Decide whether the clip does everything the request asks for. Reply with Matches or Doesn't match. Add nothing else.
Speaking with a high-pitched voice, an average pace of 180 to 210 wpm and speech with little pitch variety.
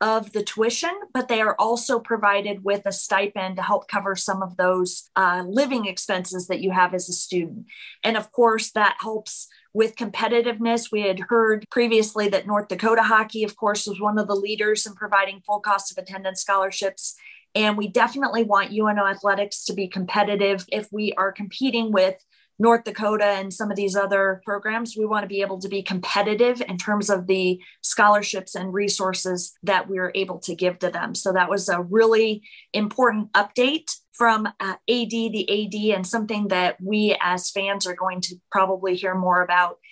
Matches